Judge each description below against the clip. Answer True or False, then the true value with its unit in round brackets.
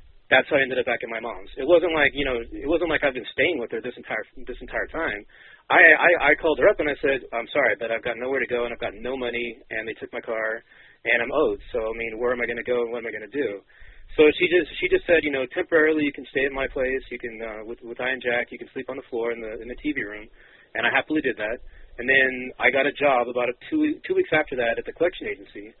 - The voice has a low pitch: True (130 Hz)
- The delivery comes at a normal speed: False (300 wpm)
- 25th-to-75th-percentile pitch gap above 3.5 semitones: True (4.6 semitones)